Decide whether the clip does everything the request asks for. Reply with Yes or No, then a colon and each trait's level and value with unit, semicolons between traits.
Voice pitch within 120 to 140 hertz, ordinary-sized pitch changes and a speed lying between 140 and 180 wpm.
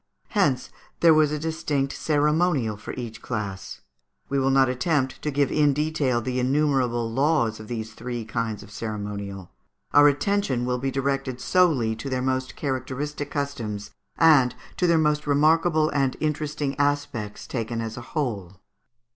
Yes: low, 135 Hz; average, 4.2 semitones; average, 155 wpm